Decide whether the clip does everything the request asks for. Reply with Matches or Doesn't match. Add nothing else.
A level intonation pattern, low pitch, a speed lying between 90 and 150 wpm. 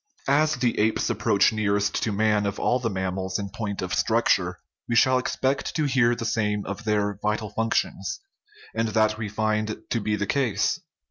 Doesn't match